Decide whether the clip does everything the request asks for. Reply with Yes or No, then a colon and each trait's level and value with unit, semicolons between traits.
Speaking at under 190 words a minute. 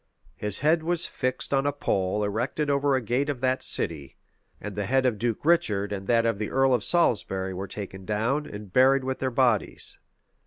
No: average, 200 wpm